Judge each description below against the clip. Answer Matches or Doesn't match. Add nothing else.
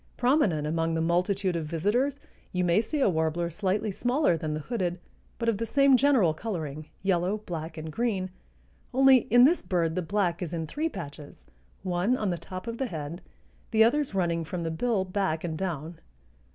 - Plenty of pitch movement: Matches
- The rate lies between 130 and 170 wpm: Doesn't match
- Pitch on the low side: Doesn't match